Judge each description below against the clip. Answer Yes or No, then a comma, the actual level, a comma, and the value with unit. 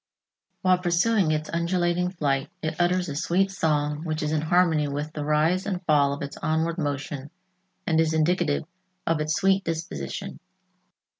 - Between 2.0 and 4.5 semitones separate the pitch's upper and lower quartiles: Yes, average, 2.9 semitones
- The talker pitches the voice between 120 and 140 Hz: No, medium, 160 Hz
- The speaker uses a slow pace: No, average, 160 wpm